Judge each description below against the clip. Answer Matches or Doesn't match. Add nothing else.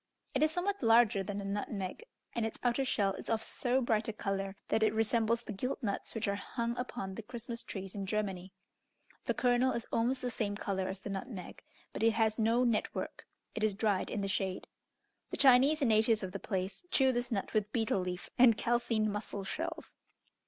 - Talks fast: Matches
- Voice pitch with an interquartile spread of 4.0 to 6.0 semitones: Doesn't match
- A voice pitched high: Matches